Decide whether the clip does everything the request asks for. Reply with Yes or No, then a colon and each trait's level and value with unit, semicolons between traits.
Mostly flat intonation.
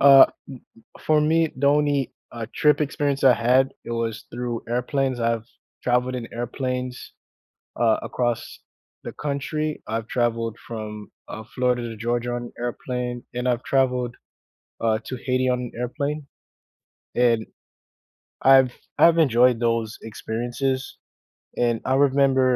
Yes: narrow, 2.2 semitones